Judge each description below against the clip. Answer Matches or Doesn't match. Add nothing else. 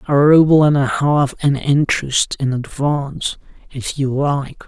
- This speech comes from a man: Matches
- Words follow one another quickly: Doesn't match